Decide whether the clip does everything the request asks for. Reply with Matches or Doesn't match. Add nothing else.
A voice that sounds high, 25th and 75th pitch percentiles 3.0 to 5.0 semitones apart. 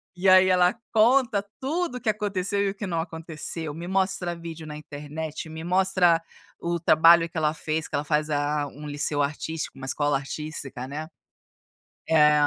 Doesn't match